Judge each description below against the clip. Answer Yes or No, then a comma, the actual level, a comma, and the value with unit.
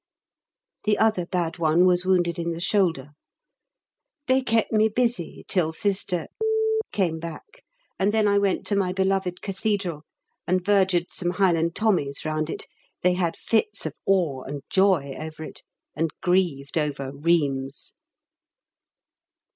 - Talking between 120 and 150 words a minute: Yes, average, 140 wpm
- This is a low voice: No, medium, 180 Hz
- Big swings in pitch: No, average, 3.6 semitones